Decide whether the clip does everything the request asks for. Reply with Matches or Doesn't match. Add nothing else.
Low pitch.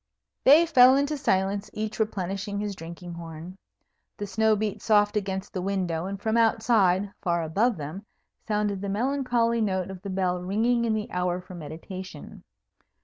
Doesn't match